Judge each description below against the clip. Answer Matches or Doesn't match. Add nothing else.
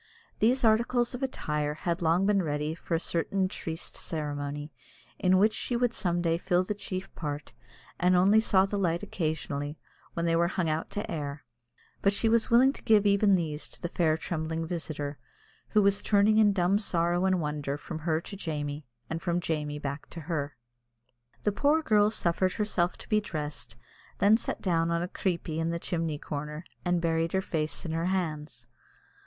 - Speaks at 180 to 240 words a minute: Matches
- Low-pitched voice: Doesn't match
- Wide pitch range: Doesn't match